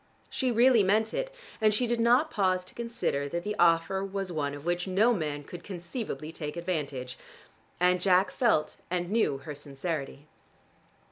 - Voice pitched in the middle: Yes, medium, 180 Hz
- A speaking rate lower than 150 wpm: No, average, 165 wpm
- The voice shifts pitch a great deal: Yes, wide, 6.0 semitones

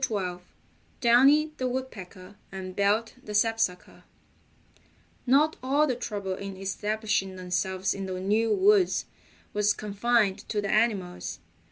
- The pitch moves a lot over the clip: No, average, 3.9 semitones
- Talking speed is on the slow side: Yes, slow, 130 wpm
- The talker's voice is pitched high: Yes, high, 210 Hz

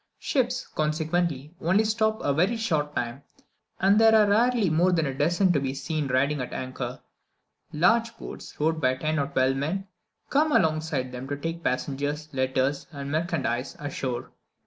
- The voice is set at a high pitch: No, medium, 155 Hz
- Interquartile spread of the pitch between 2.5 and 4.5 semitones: No, wide, 5.4 semitones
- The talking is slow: No, average, 170 wpm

